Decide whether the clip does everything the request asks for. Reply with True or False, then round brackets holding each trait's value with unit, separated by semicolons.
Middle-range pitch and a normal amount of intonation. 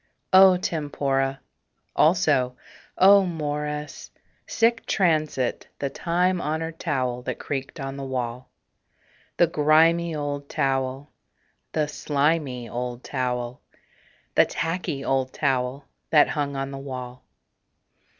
True (145 Hz; 3.5 semitones)